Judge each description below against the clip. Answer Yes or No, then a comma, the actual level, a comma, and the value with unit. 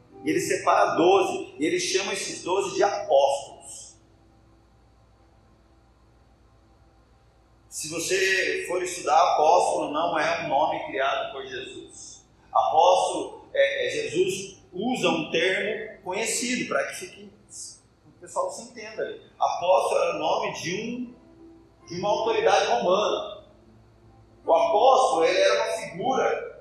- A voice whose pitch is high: No, medium, 180 Hz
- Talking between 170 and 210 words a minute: No, slow, 120 wpm